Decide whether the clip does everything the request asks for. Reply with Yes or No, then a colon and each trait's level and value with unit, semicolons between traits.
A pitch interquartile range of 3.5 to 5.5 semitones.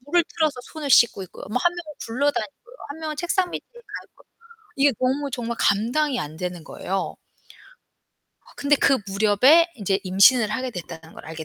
No: wide, 7.3 semitones